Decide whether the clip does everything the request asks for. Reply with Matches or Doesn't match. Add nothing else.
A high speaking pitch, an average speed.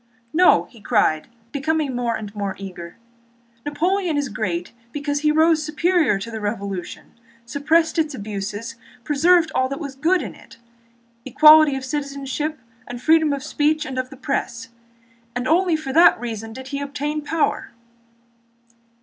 Matches